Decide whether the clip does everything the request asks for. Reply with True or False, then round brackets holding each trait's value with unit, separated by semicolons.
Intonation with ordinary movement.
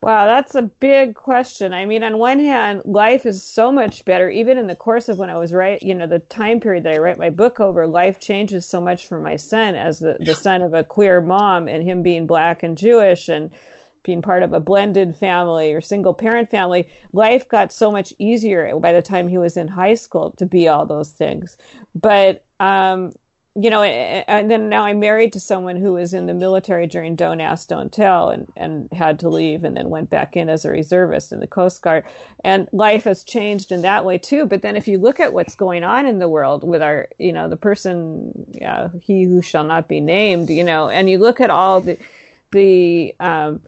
True (3.6 semitones)